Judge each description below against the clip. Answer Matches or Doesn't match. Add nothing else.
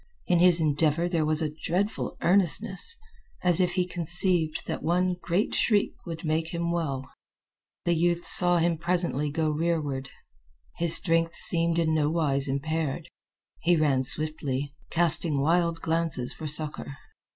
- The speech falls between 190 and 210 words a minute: Doesn't match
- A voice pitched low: Doesn't match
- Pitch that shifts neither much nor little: Doesn't match